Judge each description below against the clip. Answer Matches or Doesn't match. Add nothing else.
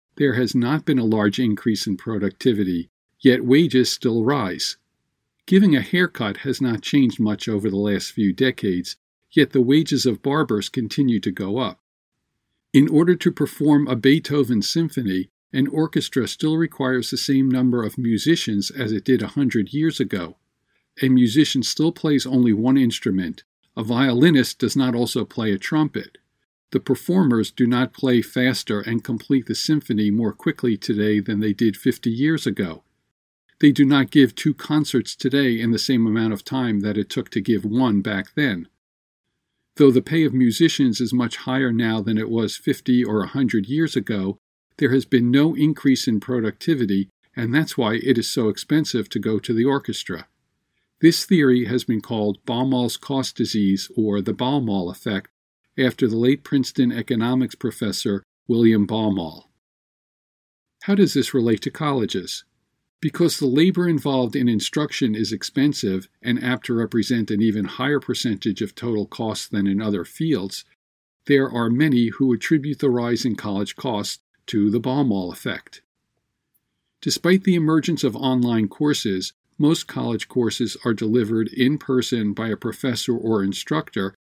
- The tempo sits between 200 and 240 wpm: Doesn't match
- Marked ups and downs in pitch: Doesn't match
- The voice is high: Doesn't match